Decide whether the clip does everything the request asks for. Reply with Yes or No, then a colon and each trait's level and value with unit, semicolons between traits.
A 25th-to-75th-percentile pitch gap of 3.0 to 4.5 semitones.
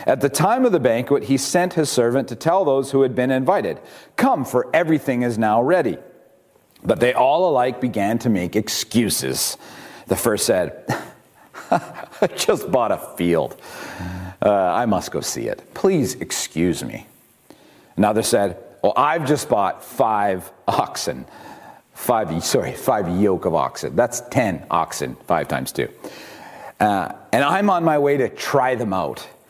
No: average, 4.9 semitones